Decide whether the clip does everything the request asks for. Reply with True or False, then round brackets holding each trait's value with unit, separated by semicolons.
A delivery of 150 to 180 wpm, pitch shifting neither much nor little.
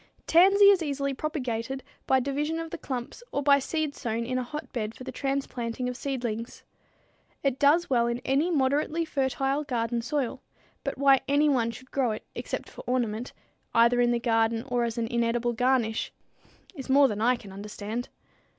True (175 wpm; 3.2 semitones)